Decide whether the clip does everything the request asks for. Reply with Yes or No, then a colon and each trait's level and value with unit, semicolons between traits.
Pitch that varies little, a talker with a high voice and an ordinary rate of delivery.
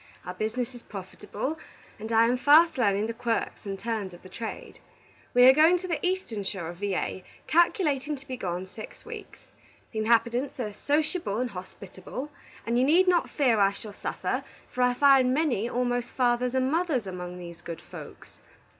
No: wide, 5.5 semitones; high, 240 Hz; average, 180 wpm